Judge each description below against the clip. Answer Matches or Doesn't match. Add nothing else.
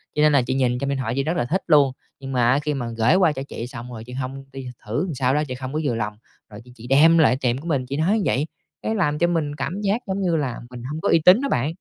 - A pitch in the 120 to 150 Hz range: Matches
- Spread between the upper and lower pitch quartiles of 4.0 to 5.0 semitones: Matches